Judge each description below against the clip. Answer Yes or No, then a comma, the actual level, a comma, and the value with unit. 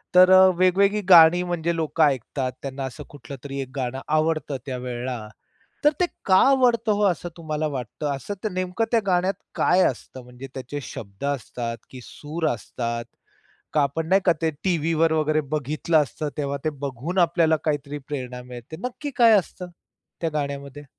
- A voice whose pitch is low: No, medium, 155 Hz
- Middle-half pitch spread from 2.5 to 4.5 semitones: No, average, 5.0 semitones